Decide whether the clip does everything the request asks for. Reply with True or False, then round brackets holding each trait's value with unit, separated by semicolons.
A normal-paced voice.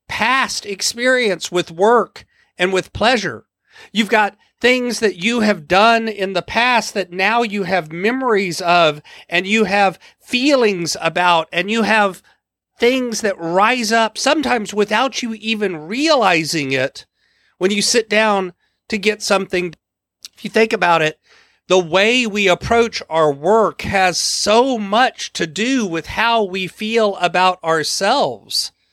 True (145 wpm)